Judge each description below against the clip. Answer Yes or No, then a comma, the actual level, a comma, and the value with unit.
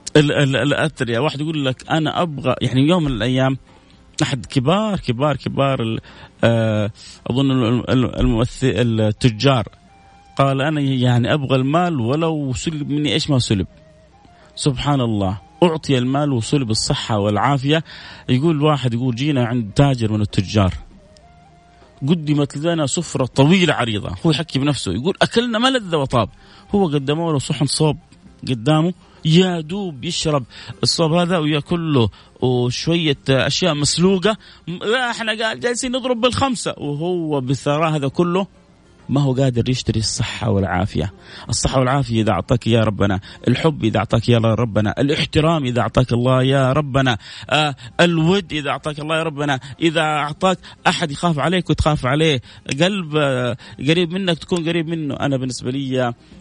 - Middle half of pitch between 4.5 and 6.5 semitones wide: Yes, average, 4.9 semitones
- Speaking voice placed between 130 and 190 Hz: Yes, medium, 140 Hz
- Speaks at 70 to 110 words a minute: No, average, 130 wpm